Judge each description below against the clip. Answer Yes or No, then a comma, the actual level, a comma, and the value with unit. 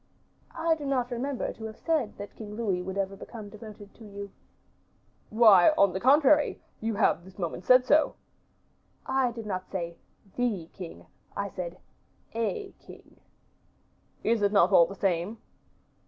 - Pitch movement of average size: Yes, average, 4.4 semitones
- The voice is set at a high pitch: Yes, high, 210 Hz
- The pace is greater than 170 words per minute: No, average, 155 wpm